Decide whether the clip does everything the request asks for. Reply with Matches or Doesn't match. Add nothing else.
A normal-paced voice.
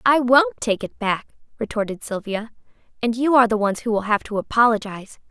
Matches